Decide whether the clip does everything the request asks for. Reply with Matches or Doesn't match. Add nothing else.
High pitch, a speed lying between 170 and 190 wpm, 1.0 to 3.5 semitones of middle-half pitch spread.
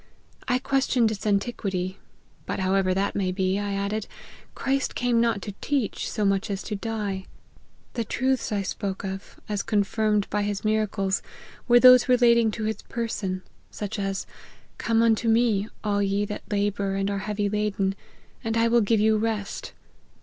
Matches